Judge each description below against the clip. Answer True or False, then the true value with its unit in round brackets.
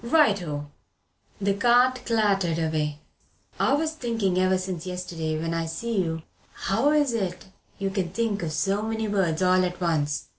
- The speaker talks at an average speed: True (170 wpm)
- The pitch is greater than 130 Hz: True (190 Hz)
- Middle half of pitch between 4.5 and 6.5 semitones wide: True (5.2 semitones)